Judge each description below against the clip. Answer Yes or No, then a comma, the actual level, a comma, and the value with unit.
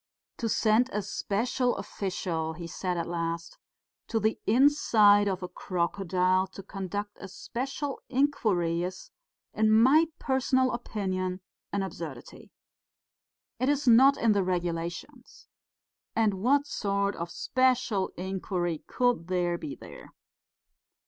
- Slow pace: Yes, slow, 120 wpm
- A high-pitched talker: Yes, high, 200 Hz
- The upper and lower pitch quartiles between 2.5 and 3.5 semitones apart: No, average, 5.3 semitones